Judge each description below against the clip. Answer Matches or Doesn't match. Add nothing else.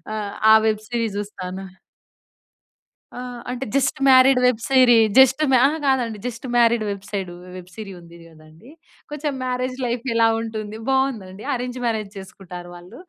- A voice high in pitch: Matches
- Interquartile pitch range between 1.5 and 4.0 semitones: Doesn't match